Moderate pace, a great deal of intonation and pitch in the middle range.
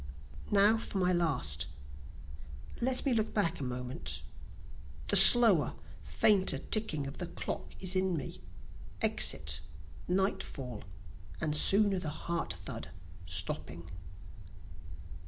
No: slow, 110 wpm; wide, 6.4 semitones; medium, 180 Hz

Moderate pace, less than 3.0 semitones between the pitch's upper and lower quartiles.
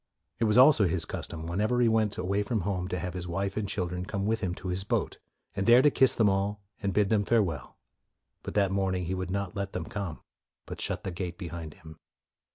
No: fast, 230 wpm; narrow, 2.6 semitones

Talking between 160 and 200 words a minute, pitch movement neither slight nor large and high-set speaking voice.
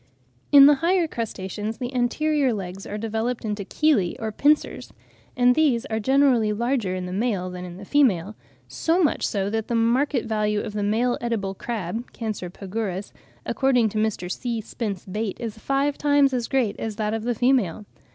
Yes: average, 180 wpm; average, 3.8 semitones; high, 225 Hz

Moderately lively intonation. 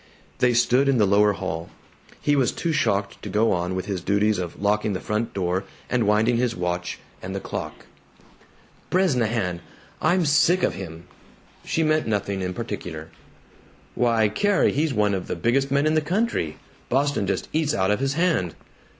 No: wide, 6.5 semitones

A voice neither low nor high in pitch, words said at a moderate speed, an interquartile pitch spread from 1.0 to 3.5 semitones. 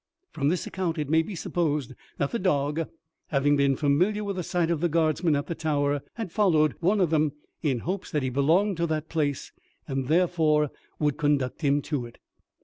Yes: medium, 155 Hz; average, 195 wpm; average, 3.2 semitones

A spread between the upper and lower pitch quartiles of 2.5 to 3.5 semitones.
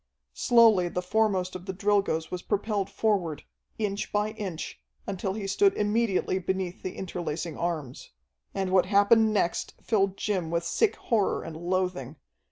Yes: average, 3.0 semitones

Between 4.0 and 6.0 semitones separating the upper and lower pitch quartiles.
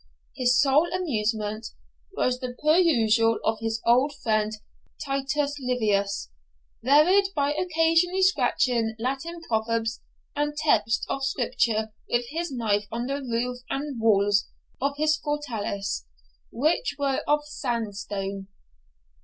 Yes: average, 5.0 semitones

